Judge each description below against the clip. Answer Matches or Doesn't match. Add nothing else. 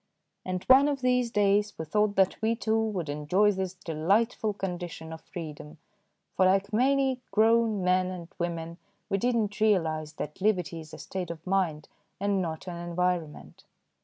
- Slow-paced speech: Doesn't match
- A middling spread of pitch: Matches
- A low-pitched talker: Doesn't match